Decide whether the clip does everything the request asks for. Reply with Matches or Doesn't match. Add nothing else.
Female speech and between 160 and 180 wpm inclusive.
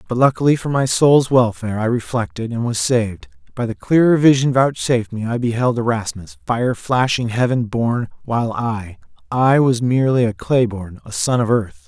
Doesn't match